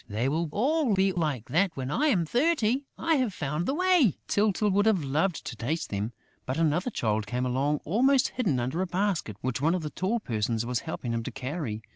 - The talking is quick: Yes, fast, 215 wpm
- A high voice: No, medium, 165 Hz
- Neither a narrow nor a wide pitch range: No, wide, 8.7 semitones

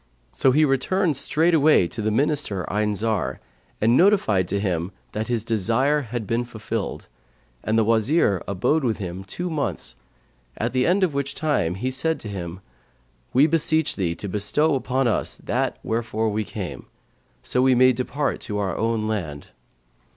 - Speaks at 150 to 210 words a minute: Yes, average, 165 wpm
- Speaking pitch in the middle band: No, low, 115 Hz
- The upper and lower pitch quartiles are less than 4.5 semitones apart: No, wide, 5.5 semitones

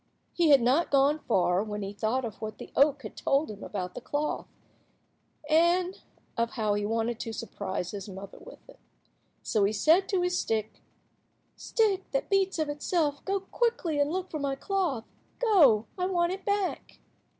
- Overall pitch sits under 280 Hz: No, very high, 285 Hz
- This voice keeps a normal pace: Yes, average, 180 wpm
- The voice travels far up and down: Yes, wide, 8.7 semitones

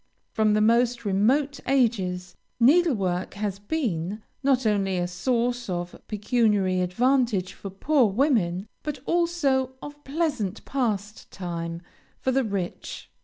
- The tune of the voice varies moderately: No, wide, 5.7 semitones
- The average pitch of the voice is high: Yes, high, 220 Hz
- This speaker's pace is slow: Yes, slow, 120 wpm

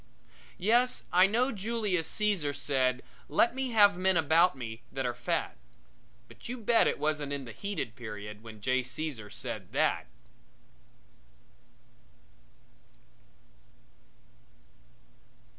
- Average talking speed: No, slow, 110 wpm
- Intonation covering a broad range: Yes, wide, 8.7 semitones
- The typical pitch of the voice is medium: Yes, medium, 155 Hz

